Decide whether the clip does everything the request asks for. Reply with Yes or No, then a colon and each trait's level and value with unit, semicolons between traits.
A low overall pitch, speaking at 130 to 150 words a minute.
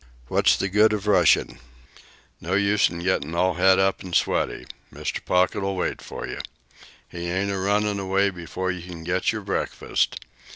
No: very low, 95 Hz; average, 170 wpm